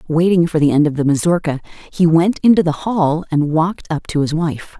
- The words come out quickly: Yes, fast, 225 wpm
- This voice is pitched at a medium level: Yes, medium, 160 Hz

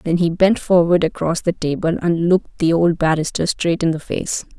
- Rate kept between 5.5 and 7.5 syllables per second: No, 5.1 syllables/s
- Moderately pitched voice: Yes, medium, 170 Hz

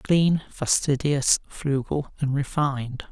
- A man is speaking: Yes, male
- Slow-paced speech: Yes, slow, 95 wpm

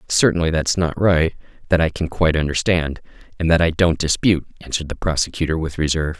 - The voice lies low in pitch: Yes, very low, 80 Hz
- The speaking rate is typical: Yes, average, 185 wpm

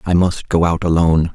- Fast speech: Yes, fast, 220 wpm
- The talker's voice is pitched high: No, very low, 85 Hz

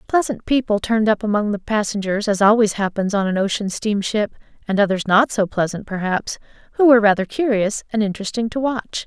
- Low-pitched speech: No, high, 210 Hz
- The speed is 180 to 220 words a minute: Yes, average, 185 wpm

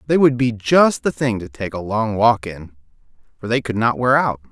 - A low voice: Yes, low, 115 Hz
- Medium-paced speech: No, fast, 240 wpm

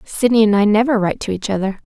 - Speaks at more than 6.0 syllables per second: Yes, 7.0 syllables/s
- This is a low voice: No, high, 210 Hz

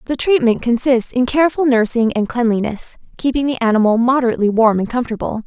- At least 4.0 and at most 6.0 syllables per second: No, 6.3 syllables/s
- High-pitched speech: Yes, high, 240 Hz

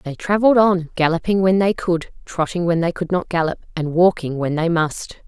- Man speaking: No, female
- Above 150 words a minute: Yes, fast, 205 wpm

